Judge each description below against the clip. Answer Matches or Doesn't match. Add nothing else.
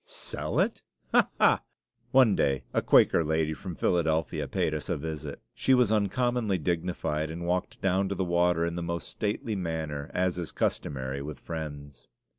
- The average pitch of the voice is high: Doesn't match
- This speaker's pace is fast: Doesn't match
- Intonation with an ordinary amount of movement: Matches